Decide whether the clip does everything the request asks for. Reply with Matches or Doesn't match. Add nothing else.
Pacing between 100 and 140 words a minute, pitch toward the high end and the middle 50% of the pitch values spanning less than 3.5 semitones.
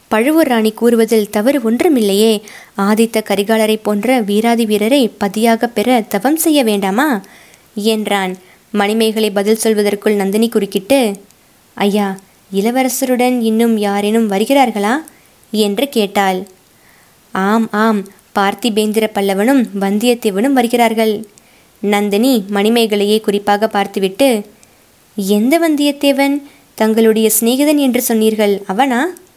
Doesn't match